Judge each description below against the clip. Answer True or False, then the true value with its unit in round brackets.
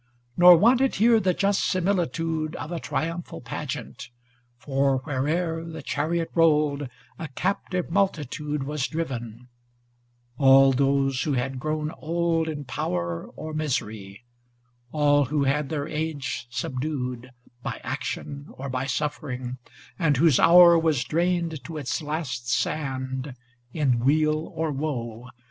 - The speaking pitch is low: False (150 Hz)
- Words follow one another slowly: True (130 wpm)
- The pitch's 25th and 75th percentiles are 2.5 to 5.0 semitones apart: True (3.8 semitones)